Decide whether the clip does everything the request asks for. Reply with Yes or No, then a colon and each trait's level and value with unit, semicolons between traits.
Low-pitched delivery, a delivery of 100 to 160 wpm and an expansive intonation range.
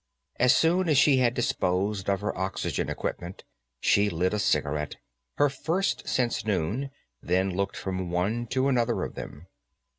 Yes: low, 105 Hz; average, 155 wpm; wide, 5.7 semitones